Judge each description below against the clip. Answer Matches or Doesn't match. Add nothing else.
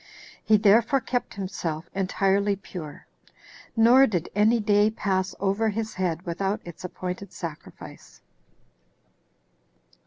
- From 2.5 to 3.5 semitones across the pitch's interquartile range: Matches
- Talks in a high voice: Matches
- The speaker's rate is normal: Doesn't match